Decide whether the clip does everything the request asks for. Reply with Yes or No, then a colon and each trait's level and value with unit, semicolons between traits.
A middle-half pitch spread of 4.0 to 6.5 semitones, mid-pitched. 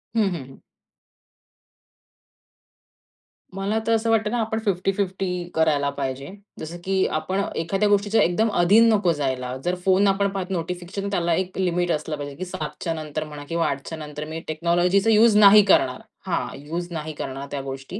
Yes: average, 4.6 semitones; medium, 175 Hz